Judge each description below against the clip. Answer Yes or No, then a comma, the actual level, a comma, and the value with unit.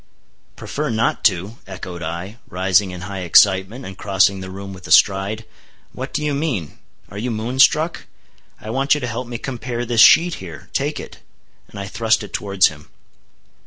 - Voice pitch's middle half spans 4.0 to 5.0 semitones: Yes, average, 4.4 semitones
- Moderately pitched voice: No, low, 105 Hz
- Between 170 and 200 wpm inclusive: Yes, average, 180 wpm